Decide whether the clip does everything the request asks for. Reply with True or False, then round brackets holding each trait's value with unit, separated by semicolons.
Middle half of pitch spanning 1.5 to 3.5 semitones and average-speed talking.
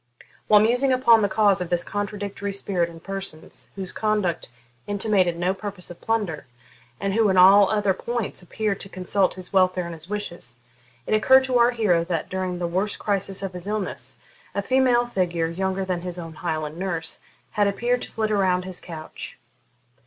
True (2.9 semitones; 180 wpm)